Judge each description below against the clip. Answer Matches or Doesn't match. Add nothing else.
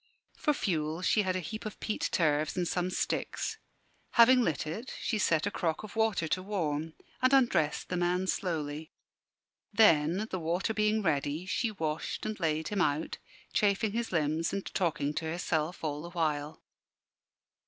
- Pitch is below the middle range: Doesn't match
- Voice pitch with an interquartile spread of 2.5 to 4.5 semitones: Doesn't match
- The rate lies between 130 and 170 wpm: Matches